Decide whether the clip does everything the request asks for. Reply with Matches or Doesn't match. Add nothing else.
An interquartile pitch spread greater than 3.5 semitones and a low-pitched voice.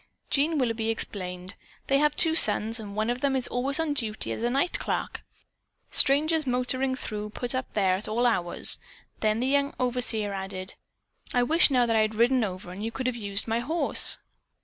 Doesn't match